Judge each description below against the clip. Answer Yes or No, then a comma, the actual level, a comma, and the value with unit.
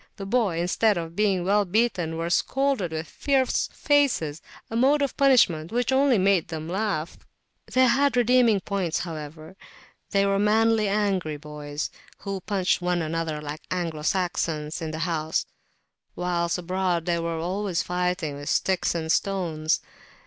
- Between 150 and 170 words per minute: Yes, average, 155 wpm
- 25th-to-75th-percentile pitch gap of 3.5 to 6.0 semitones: Yes, average, 4.6 semitones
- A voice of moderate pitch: Yes, medium, 180 Hz